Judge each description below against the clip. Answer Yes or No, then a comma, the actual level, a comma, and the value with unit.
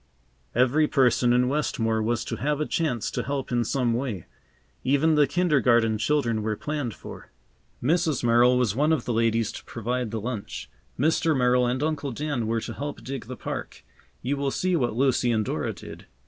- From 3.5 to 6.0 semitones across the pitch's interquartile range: Yes, average, 3.9 semitones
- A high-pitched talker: No, low, 125 Hz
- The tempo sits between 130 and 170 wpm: No, average, 190 wpm